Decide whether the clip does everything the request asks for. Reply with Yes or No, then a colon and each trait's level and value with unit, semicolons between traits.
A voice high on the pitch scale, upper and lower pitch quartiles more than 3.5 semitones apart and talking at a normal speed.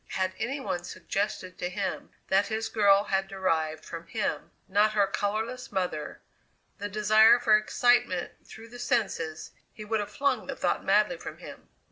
No: high, 205 Hz; average, 3.0 semitones; average, 165 wpm